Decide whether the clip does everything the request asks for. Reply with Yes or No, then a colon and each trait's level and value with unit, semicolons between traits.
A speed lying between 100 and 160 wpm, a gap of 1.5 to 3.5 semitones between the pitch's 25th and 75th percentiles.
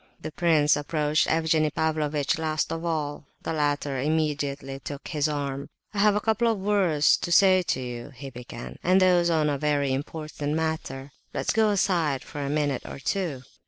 No: average, 180 wpm; average, 2.9 semitones